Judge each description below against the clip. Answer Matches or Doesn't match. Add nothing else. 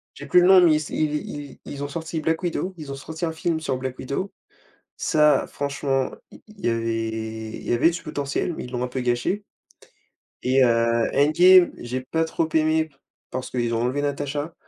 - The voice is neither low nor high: Matches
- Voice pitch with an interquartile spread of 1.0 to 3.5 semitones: Doesn't match